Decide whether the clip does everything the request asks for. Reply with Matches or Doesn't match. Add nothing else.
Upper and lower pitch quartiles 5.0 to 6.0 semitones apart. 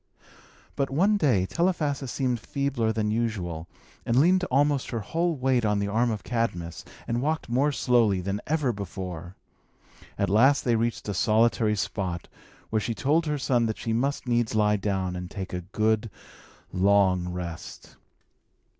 Matches